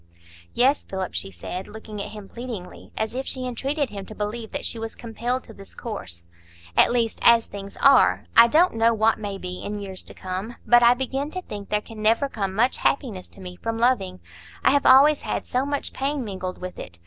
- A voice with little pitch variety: No, average, 4.2 semitones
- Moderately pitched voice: No, high, 225 Hz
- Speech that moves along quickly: Yes, fast, 220 wpm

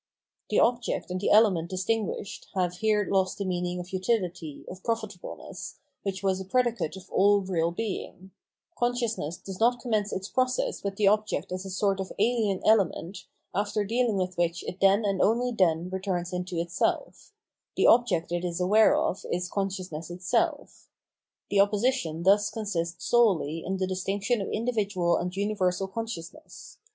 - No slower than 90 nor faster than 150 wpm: No, average, 165 wpm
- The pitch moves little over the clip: No, average, 3.3 semitones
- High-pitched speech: Yes, high, 195 Hz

